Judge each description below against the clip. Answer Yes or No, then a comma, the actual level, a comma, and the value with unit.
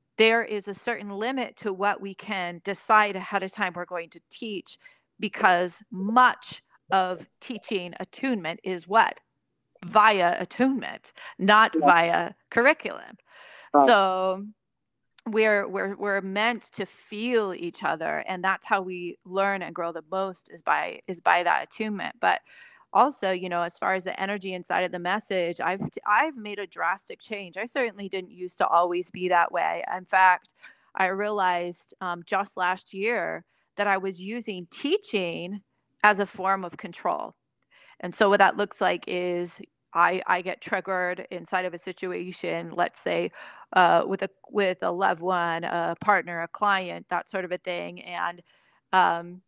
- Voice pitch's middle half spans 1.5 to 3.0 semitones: Yes, average, 2.7 semitones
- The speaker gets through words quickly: No, average, 160 wpm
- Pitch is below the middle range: No, high, 190 Hz